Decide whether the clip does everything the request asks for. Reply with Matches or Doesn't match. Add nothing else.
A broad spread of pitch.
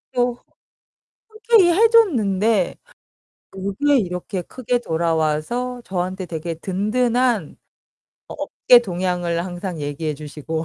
Matches